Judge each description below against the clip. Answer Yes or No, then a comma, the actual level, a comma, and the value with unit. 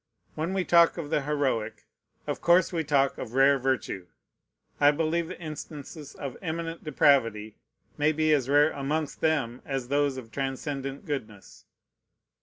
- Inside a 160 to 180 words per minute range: No, average, 150 wpm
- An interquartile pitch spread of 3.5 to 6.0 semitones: No, average, 2.9 semitones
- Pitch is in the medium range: Yes, medium, 145 Hz